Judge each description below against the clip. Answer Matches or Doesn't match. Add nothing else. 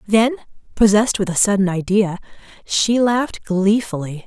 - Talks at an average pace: Doesn't match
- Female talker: Matches